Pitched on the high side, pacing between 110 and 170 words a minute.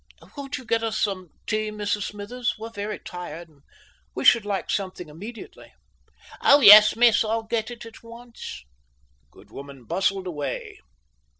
Yes: high, 210 Hz; average, 155 wpm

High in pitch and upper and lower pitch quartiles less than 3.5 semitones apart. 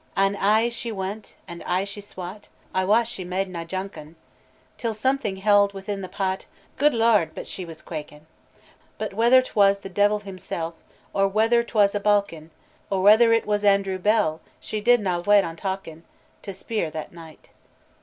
Yes: high, 200 Hz; narrow, 2.5 semitones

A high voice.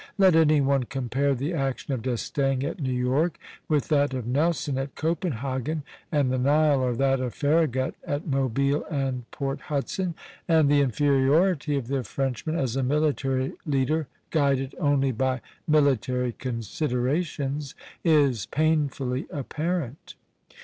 No: medium, 140 Hz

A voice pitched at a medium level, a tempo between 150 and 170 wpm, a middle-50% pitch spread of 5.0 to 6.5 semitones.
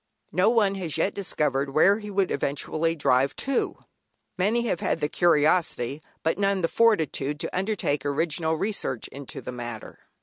Yes: medium, 165 Hz; average, 160 wpm; wide, 5.6 semitones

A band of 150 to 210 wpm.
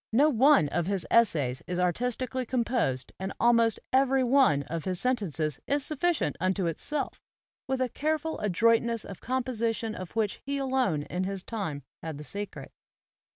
Yes: average, 160 wpm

